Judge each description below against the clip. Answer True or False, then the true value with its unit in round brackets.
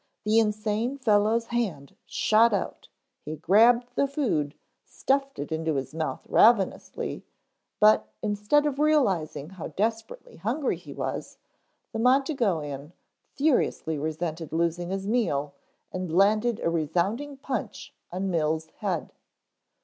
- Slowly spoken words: True (120 wpm)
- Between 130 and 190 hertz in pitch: False (205 Hz)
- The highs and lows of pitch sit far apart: True (6.8 semitones)